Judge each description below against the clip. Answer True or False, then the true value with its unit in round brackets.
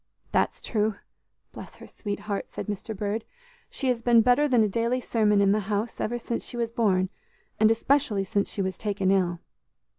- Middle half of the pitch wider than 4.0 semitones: False (2.6 semitones)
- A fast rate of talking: False (190 wpm)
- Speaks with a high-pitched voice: True (215 Hz)